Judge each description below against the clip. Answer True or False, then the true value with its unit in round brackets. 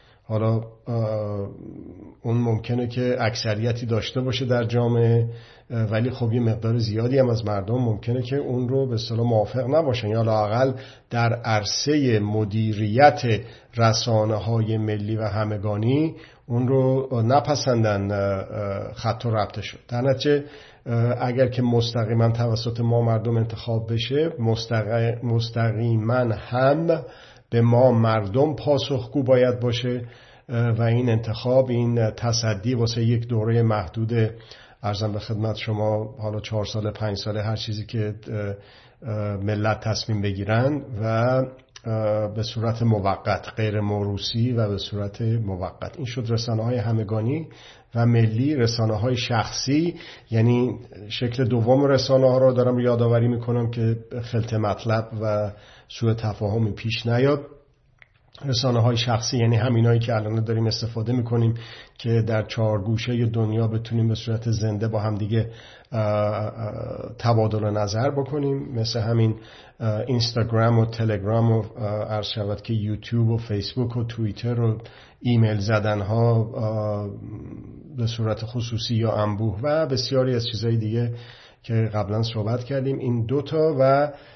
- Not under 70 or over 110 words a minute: False (130 wpm)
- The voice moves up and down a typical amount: False (2.1 semitones)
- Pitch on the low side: True (115 Hz)